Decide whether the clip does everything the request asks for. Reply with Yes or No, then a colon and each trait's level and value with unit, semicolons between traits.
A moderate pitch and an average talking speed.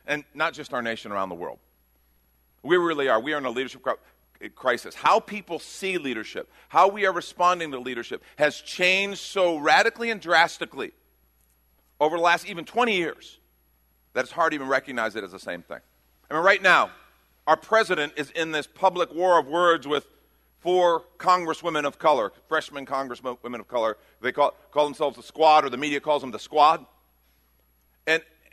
Yes: medium, 150 Hz; average, 180 wpm